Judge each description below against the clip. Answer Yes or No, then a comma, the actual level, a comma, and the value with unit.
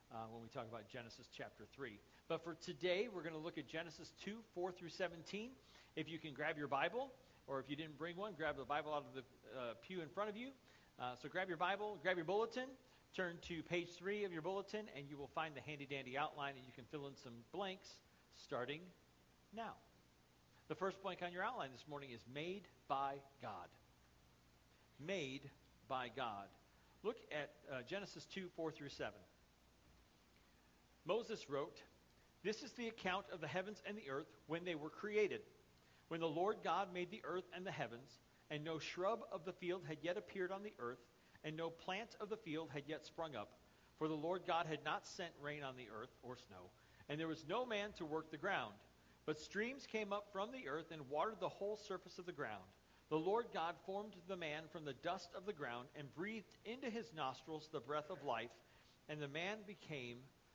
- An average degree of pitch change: No, wide, 5.7 semitones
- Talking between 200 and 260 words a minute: Yes, fast, 205 wpm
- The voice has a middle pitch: Yes, medium, 160 Hz